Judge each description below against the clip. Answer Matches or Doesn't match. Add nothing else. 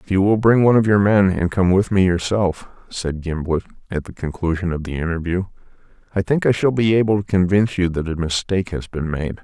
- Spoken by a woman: Doesn't match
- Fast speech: Matches